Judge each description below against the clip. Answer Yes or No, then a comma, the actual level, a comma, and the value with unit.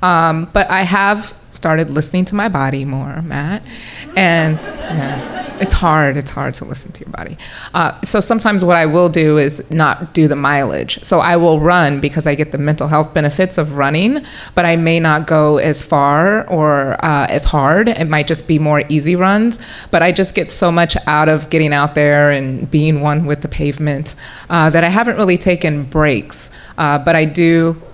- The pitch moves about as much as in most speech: Yes, average, 3.1 semitones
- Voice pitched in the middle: Yes, medium, 160 Hz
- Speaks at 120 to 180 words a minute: No, average, 200 wpm